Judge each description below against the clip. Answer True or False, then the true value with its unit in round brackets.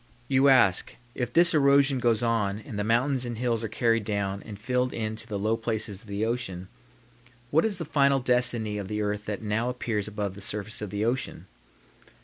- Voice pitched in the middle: False (115 Hz)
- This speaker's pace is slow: False (205 wpm)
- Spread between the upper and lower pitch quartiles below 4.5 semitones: True (3.3 semitones)